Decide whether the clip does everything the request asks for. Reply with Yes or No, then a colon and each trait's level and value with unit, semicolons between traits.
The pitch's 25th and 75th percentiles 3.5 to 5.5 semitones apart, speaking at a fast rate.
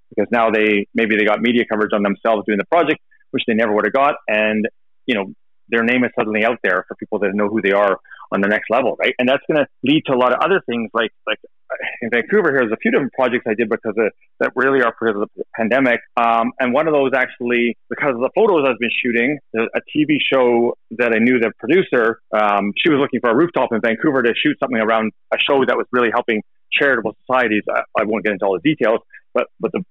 No: average, 3.0 semitones; fast, 250 wpm